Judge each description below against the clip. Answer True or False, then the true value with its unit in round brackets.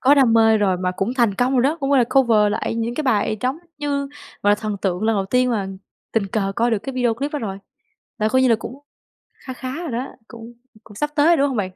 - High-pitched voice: True (235 Hz)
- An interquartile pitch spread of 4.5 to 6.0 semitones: False (4.0 semitones)